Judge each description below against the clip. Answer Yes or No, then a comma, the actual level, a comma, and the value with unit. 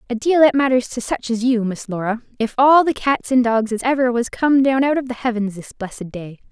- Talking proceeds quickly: Yes, fast, 260 wpm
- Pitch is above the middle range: Yes, high, 245 Hz